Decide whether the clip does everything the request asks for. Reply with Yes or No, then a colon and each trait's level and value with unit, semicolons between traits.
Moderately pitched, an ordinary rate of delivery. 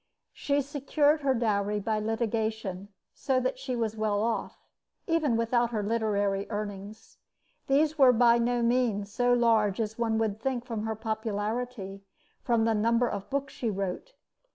No: high, 225 Hz; average, 160 wpm